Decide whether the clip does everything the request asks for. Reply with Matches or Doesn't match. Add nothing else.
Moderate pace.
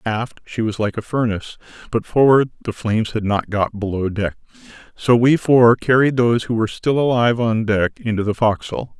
Matches